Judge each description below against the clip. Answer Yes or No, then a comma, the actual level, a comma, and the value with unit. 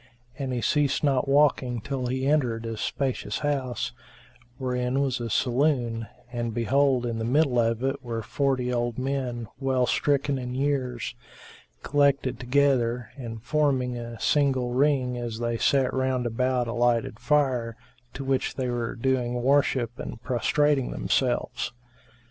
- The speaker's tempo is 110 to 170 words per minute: Yes, average, 145 wpm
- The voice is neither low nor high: No, low, 125 Hz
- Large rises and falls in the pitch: No, narrow, 2.4 semitones